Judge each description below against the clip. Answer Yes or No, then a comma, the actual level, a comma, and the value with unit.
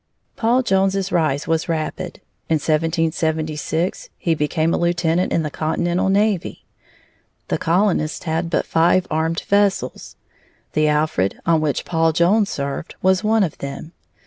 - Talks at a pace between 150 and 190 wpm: No, average, 140 wpm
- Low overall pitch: No, medium, 165 Hz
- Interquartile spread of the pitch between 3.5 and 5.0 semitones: No, average, 3.0 semitones